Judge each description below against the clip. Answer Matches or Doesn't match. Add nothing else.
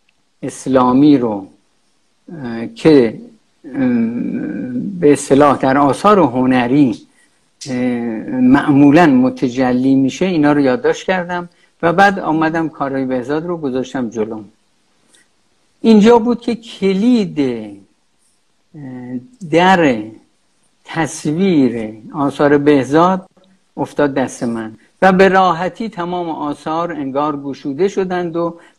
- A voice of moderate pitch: Matches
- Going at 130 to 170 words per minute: Doesn't match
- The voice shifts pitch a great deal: Matches